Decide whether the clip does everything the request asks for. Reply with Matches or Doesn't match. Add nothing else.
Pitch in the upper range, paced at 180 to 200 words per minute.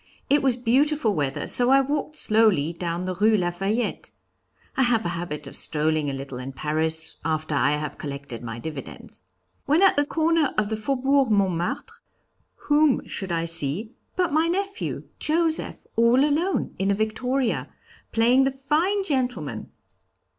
Doesn't match